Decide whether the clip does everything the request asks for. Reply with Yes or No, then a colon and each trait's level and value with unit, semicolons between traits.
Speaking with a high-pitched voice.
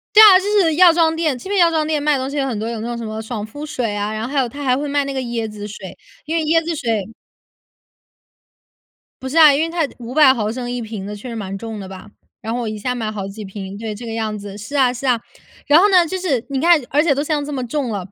Yes: very high, 250 Hz